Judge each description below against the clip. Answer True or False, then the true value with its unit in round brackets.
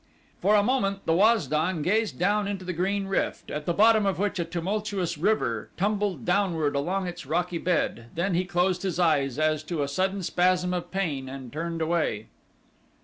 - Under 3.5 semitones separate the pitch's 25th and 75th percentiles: False (3.8 semitones)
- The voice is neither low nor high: True (180 Hz)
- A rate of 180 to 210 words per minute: True (190 wpm)